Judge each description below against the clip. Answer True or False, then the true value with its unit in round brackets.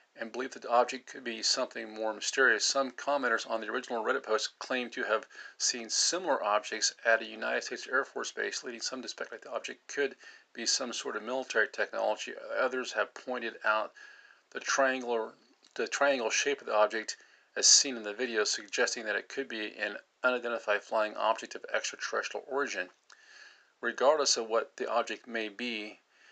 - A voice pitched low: True (115 Hz)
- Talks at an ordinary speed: True (180 wpm)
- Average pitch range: True (3.0 semitones)